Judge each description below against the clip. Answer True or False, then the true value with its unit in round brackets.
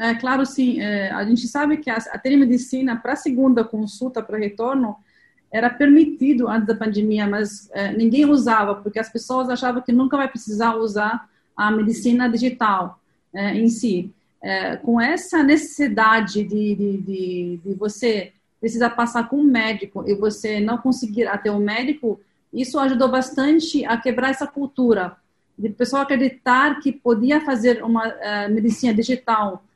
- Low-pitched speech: False (230 Hz)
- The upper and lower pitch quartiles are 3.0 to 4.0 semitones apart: True (3.6 semitones)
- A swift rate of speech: False (160 wpm)